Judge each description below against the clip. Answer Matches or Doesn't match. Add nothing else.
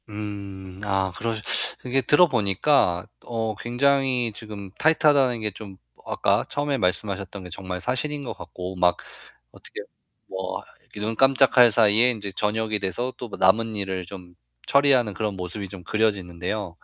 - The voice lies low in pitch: Matches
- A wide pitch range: Doesn't match